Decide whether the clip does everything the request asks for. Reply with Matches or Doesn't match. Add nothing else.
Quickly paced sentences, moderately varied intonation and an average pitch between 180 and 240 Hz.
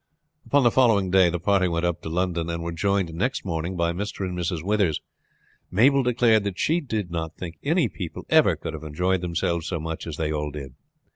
Doesn't match